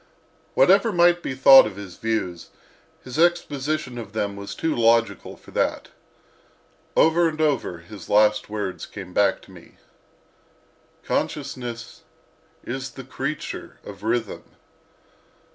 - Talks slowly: Yes, slow, 125 wpm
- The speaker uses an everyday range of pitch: No, wide, 6.4 semitones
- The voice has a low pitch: Yes, low, 120 Hz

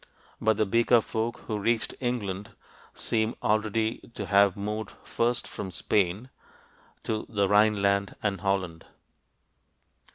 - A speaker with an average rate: No, slow, 120 wpm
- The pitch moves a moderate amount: No, narrow, 2.0 semitones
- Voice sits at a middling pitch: No, low, 105 Hz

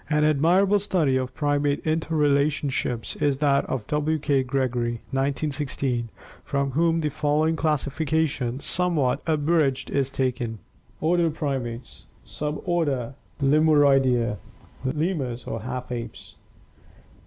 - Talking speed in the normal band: No, slow, 105 wpm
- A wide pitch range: No, average, 3.1 semitones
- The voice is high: No, medium, 145 Hz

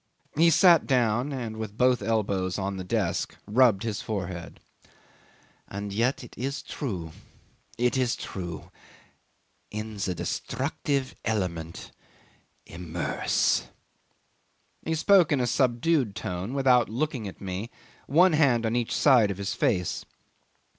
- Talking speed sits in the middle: No, slow, 125 wpm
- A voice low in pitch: Yes, low, 115 Hz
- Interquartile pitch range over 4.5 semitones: Yes, average, 5.1 semitones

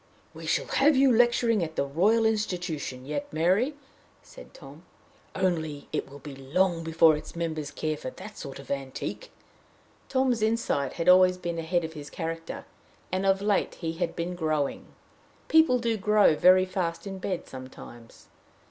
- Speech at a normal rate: Yes, average, 165 wpm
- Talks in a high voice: No, medium, 175 Hz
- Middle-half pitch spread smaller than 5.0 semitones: No, average, 5.3 semitones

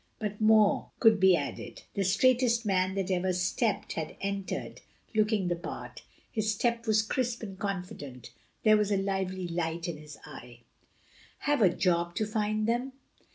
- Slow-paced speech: No, average, 160 wpm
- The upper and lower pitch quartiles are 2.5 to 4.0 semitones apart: Yes, average, 3.5 semitones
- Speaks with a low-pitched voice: No, high, 200 Hz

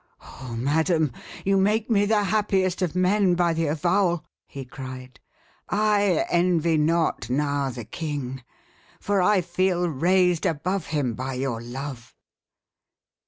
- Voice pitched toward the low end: No, medium, 165 Hz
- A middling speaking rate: No, slow, 130 wpm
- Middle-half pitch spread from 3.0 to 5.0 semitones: No, wide, 5.4 semitones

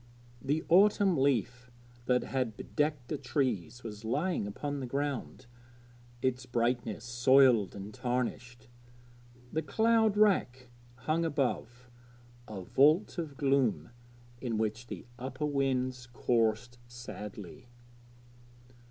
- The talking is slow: Yes, slow, 110 wpm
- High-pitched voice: No, low, 125 Hz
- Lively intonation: No, average, 3.2 semitones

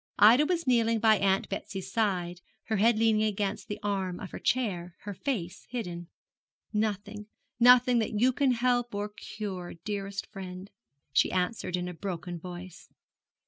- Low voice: No, high, 205 Hz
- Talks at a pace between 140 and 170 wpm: Yes, average, 155 wpm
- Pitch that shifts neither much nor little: Yes, average, 3.7 semitones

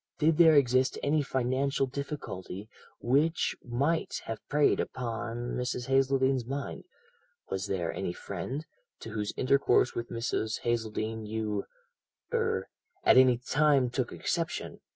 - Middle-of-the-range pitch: No, low, 125 Hz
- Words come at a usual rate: No, slow, 125 wpm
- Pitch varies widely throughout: No, average, 3.7 semitones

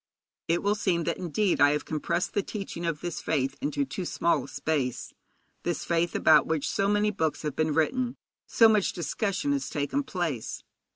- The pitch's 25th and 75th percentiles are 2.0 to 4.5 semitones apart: No, average, 5.1 semitones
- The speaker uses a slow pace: No, average, 185 wpm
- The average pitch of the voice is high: No, medium, 170 Hz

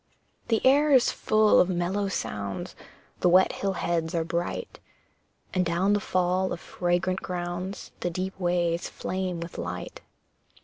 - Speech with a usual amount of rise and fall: No, narrow, 1.9 semitones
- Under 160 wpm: Yes, average, 145 wpm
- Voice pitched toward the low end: No, medium, 180 Hz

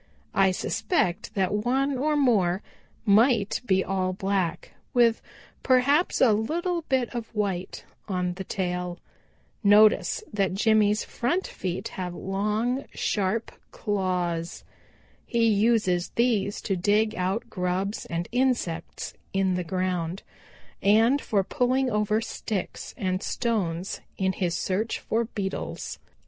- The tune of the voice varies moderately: Yes, average, 4.0 semitones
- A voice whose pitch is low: No, high, 205 Hz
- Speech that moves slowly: Yes, slow, 120 wpm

